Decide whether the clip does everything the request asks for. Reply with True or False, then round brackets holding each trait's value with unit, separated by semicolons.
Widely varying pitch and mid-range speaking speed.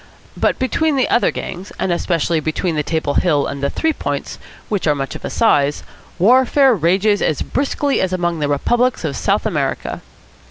True (7.9 semitones; 185 wpm)